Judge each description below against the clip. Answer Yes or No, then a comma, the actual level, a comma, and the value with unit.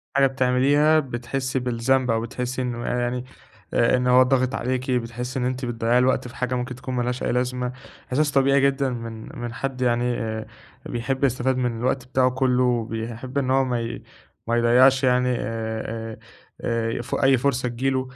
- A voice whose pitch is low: Yes, low, 125 Hz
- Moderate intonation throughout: No, narrow, 1.6 semitones